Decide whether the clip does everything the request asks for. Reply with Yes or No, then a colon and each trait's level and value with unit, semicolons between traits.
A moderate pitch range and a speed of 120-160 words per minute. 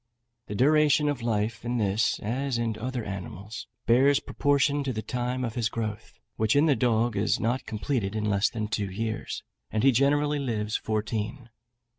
No: average, 3.7 semitones; average, 175 wpm